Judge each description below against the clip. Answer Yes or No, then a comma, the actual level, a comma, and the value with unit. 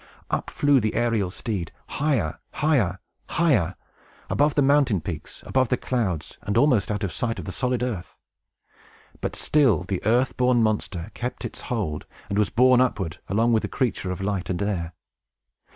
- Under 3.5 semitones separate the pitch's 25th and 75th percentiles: No, average, 5.2 semitones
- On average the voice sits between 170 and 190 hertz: No, low, 110 Hz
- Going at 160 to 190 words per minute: Yes, average, 170 wpm